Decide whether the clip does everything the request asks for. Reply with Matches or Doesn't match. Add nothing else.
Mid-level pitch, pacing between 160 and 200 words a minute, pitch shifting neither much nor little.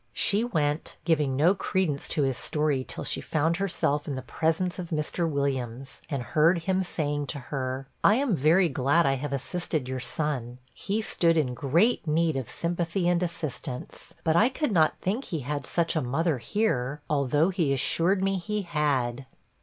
Matches